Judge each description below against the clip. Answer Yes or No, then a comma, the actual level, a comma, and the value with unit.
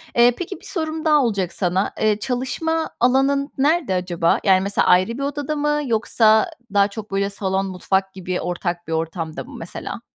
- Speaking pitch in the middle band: No, high, 215 Hz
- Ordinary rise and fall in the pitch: No, wide, 6.9 semitones